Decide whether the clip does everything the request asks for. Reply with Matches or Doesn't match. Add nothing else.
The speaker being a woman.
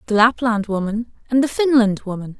Matches